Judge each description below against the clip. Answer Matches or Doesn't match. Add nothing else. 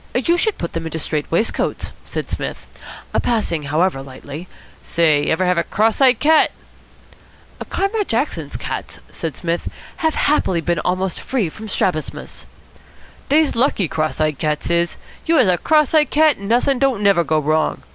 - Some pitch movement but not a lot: Doesn't match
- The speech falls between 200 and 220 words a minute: Doesn't match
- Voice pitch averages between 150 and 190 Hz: Matches